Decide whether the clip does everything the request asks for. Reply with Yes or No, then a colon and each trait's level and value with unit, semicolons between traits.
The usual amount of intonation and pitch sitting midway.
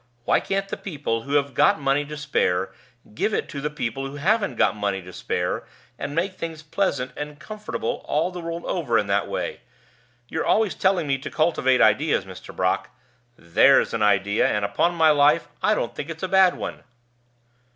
No: wide, 6.6 semitones; medium, 145 Hz